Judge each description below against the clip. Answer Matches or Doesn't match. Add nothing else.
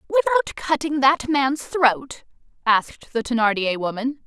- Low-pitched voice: Doesn't match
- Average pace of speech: Doesn't match